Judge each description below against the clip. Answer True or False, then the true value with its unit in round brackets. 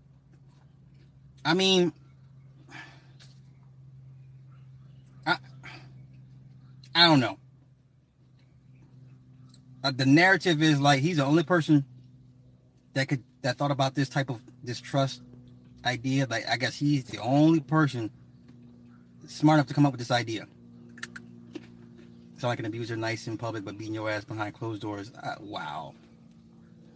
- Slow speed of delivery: True (120 wpm)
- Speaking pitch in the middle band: False (130 Hz)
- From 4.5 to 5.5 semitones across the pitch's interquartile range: False (2.4 semitones)